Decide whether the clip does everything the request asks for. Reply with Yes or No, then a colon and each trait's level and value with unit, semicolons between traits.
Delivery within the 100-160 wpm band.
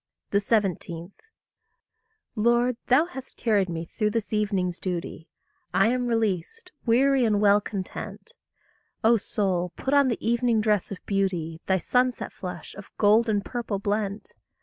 Yes: average, 140 wpm